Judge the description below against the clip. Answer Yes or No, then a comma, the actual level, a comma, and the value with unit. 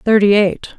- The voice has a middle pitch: No, high, 205 Hz